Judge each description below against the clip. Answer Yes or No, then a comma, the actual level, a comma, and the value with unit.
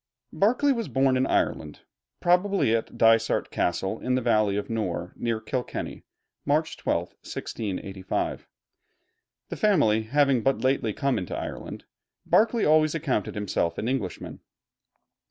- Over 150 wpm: No, slow, 135 wpm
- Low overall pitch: Yes, low, 125 Hz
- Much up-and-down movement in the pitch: Yes, wide, 6.2 semitones